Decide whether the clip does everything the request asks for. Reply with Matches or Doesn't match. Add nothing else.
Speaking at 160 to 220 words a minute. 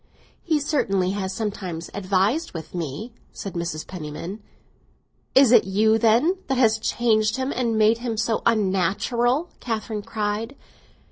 Doesn't match